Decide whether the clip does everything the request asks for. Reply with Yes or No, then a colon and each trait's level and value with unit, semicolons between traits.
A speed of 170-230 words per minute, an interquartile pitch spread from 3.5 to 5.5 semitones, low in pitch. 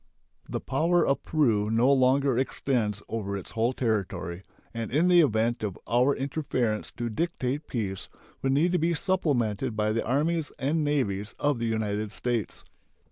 No: average, 160 wpm; average, 5.0 semitones; low, 125 Hz